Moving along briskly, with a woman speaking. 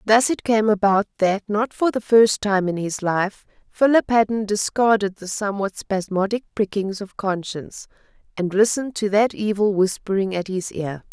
No: average, 165 wpm; female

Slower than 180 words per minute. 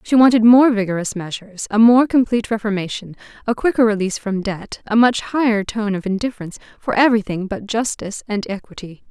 Yes: average, 170 wpm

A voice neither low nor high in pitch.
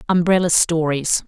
Yes: medium, 165 Hz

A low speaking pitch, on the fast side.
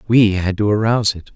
Yes: low, 105 Hz; fast, 220 wpm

